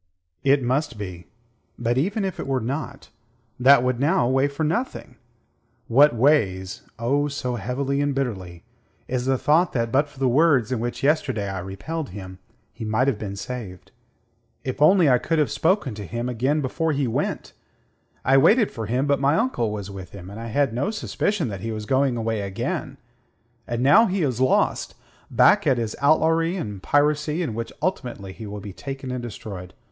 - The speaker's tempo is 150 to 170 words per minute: No, average, 190 wpm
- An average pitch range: Yes, average, 4.7 semitones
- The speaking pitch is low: Yes, low, 130 Hz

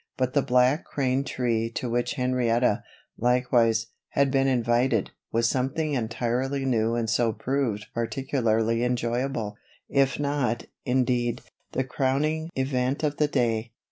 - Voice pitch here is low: Yes, low, 125 Hz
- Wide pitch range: No, narrow, 2.5 semitones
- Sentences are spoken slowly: Yes, slow, 130 wpm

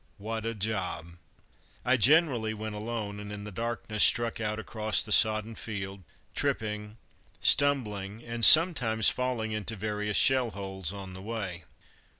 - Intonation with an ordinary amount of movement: No, narrow, 2.2 semitones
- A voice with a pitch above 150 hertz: No, low, 110 Hz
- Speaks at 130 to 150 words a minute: Yes, average, 145 wpm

